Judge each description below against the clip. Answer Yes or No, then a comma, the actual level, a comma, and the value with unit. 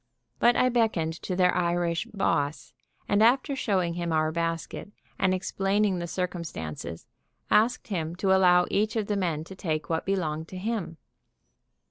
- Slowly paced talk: No, average, 155 wpm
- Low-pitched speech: No, medium, 180 Hz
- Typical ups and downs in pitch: Yes, average, 3.5 semitones